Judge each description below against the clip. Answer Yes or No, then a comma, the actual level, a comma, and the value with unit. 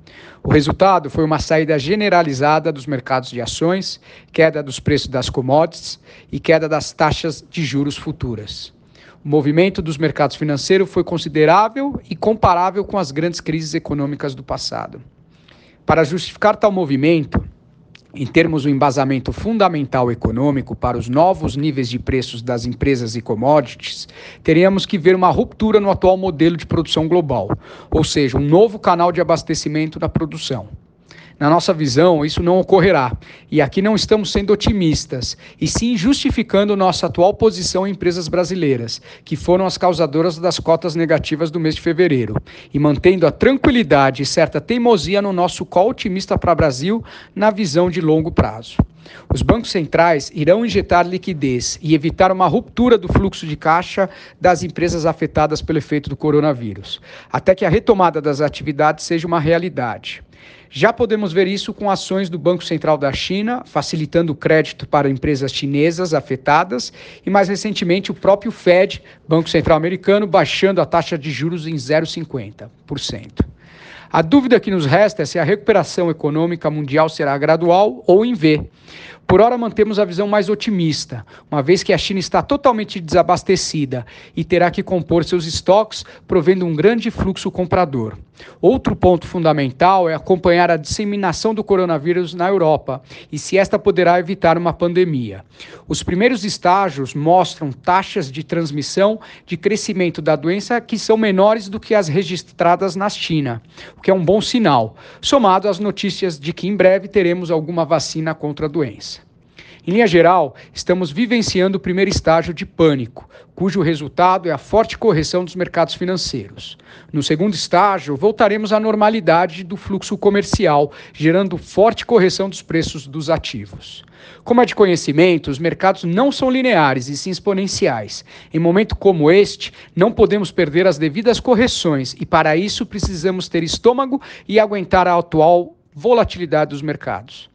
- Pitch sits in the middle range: Yes, medium, 175 Hz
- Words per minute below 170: Yes, average, 155 wpm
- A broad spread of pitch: No, average, 4.2 semitones